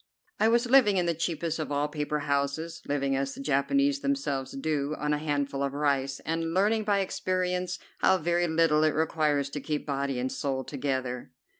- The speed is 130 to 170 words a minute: No, average, 185 wpm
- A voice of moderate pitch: Yes, medium, 150 Hz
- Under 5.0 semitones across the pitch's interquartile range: Yes, average, 3.9 semitones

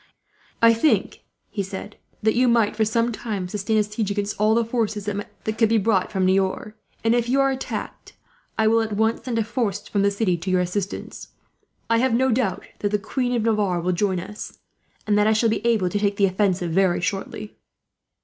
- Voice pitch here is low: No, high, 210 Hz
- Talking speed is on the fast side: Yes, fast, 215 wpm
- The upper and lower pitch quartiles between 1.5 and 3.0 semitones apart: Yes, narrow, 2.6 semitones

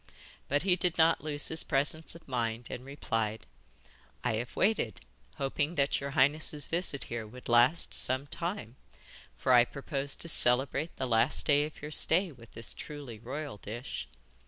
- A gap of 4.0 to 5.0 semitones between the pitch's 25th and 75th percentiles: Yes, average, 4.4 semitones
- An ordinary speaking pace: Yes, average, 165 wpm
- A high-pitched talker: No, medium, 140 Hz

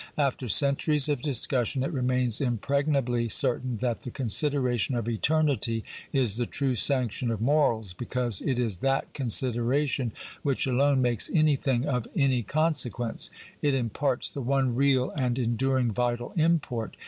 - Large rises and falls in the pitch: No, average, 2.7 semitones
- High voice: No, low, 130 Hz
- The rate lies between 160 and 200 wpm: No, average, 145 wpm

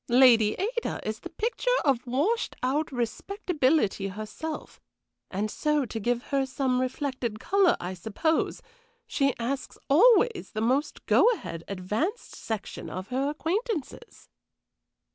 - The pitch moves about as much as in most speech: No, wide, 6.8 semitones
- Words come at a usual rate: No, slow, 125 wpm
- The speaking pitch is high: Yes, very high, 270 Hz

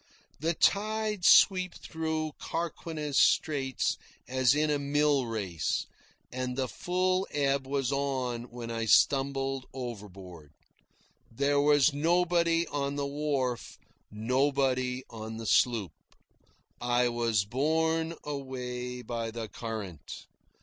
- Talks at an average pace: No, slow, 110 wpm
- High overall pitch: No, low, 135 Hz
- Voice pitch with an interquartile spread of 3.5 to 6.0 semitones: Yes, average, 4.0 semitones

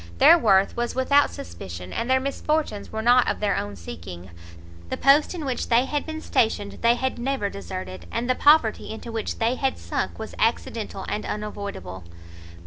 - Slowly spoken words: No, average, 180 wpm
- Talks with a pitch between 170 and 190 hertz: No, high, 230 Hz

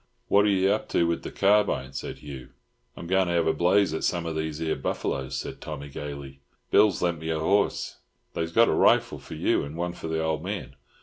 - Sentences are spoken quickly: Yes, fast, 230 wpm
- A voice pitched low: Yes, very low, 80 Hz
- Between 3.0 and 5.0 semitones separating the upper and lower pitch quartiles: Yes, average, 3.8 semitones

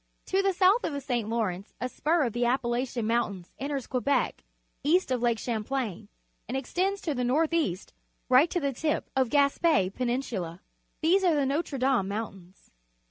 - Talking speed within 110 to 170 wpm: No, average, 180 wpm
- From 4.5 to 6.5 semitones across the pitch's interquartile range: Yes, average, 4.9 semitones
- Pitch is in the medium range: No, very high, 255 Hz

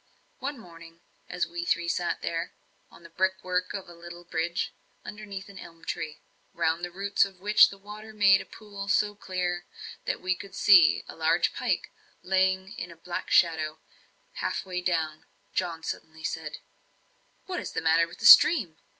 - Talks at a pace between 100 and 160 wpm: No, average, 175 wpm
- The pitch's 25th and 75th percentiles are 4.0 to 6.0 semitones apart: No, average, 2.9 semitones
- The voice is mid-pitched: Yes, medium, 180 Hz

